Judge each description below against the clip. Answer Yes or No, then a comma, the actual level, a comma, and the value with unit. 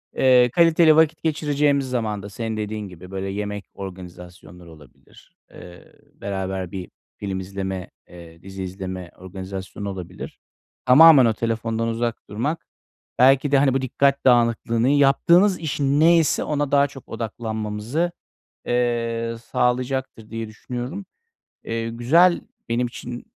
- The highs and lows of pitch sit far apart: Yes, wide, 5.9 semitones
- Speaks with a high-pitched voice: No, low, 115 Hz